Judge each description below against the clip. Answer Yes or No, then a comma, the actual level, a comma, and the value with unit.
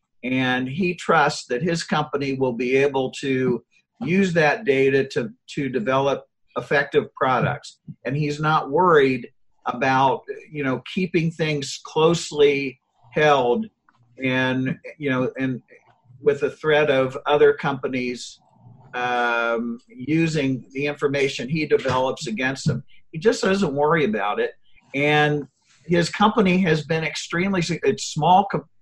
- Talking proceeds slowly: Yes, slow, 130 wpm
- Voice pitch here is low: No, medium, 145 Hz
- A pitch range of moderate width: Yes, average, 4.1 semitones